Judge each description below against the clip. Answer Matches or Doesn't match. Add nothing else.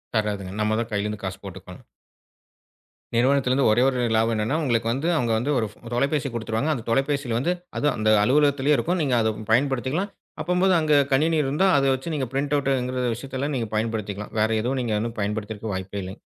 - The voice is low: Matches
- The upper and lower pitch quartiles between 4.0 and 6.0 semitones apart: Matches